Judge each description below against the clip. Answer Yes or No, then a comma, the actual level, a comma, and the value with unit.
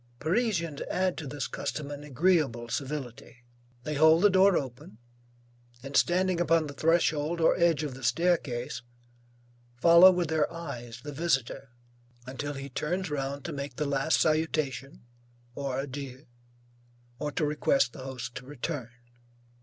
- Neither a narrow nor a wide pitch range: Yes, average, 3.7 semitones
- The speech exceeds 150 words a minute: No, average, 145 wpm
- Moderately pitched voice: Yes, medium, 145 Hz